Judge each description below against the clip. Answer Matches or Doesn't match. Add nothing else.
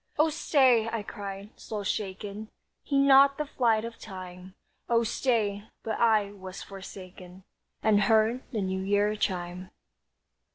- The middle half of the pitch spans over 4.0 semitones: Doesn't match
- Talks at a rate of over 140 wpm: Doesn't match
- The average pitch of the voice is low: Doesn't match